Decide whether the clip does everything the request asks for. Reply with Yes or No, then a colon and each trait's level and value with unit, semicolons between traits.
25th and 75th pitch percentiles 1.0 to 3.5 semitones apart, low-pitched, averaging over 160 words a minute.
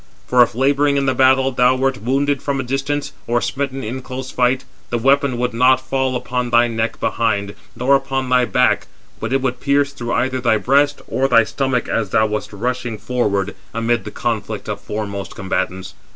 Yes: narrow, 2.6 semitones; low, 125 Hz; average, 195 wpm